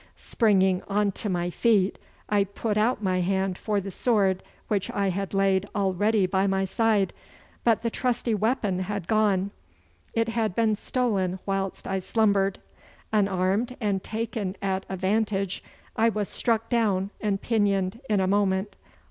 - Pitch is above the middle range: Yes, high, 200 Hz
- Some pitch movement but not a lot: No, narrow, 2.3 semitones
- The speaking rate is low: No, average, 155 wpm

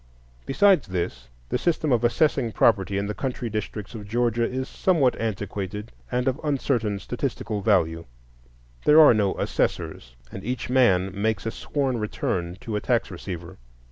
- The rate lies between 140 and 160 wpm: Yes, average, 155 wpm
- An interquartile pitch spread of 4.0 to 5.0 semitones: Yes, average, 4.4 semitones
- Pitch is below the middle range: Yes, low, 110 Hz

